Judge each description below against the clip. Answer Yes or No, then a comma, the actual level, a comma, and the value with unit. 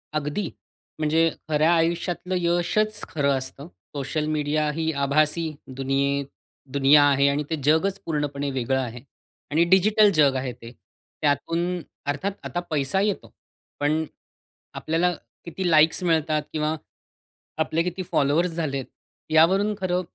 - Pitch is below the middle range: No, medium, 155 Hz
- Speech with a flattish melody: No, average, 3.3 semitones